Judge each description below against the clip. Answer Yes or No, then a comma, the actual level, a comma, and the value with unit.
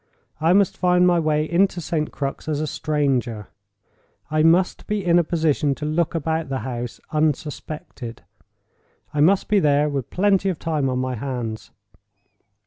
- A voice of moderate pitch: Yes, medium, 155 Hz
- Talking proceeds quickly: No, average, 150 wpm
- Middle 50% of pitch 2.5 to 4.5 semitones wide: Yes, average, 4.2 semitones